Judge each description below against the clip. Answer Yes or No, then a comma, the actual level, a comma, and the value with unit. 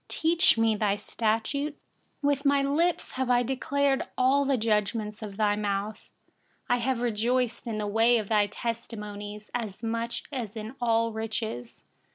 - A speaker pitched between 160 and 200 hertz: No, high, 230 Hz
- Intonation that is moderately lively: Yes, average, 3.4 semitones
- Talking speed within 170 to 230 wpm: No, average, 155 wpm